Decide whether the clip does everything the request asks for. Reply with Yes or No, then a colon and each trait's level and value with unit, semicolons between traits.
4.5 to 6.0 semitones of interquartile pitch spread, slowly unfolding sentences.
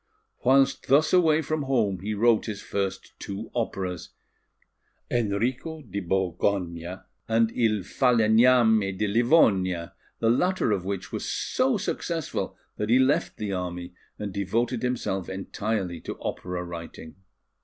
Yes: average, 4.8 semitones; slow, 130 wpm